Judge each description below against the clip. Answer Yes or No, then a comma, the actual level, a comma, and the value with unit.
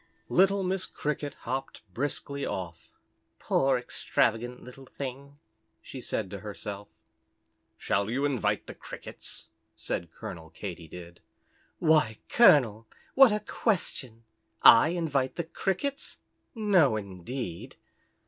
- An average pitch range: No, wide, 7.4 semitones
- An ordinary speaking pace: No, slow, 110 wpm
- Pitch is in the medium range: No, low, 130 Hz